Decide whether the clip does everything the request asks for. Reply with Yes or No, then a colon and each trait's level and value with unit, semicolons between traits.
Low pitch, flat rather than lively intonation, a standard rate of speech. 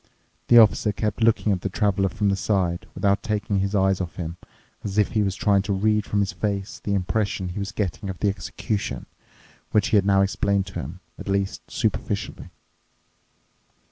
Yes: low, 100 Hz; narrow, 1.5 semitones; average, 190 wpm